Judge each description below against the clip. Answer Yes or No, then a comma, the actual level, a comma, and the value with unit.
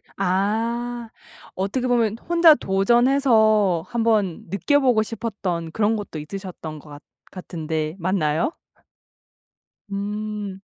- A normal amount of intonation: Yes, average, 4.2 semitones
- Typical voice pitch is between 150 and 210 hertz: Yes, high, 205 Hz